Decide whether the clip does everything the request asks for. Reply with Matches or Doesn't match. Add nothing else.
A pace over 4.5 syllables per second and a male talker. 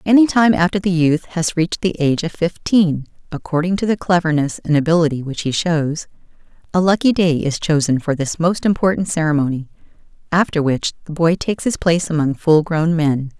Doesn't match